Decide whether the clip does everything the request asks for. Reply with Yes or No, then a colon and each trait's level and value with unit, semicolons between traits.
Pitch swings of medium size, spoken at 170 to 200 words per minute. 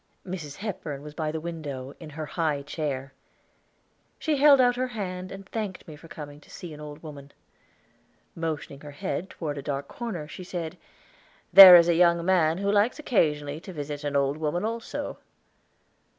Yes: average, 4.3 semitones; average, 180 wpm